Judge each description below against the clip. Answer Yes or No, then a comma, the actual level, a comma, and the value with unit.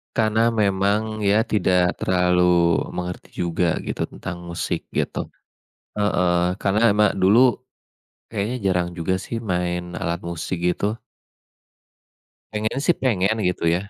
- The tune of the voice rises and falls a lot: No, average, 3.3 semitones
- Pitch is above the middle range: No, very low, 95 Hz